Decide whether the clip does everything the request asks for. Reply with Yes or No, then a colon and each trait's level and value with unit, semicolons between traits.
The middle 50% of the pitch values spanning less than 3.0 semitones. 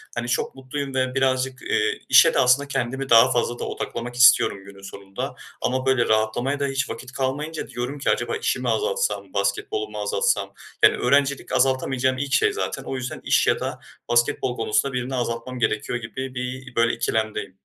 Yes: narrow, 2.5 semitones